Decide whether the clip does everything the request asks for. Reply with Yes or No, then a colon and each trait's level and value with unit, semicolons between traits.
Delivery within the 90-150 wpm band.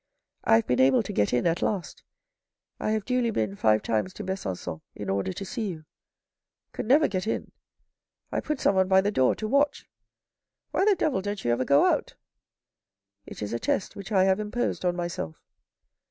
No: fast, 205 wpm